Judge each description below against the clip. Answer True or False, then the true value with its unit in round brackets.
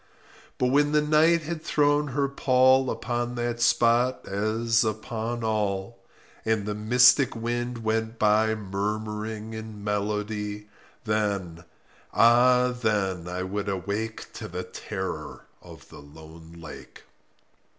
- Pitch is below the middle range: True (110 Hz)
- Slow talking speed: True (120 wpm)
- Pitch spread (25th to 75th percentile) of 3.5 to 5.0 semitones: False (2.8 semitones)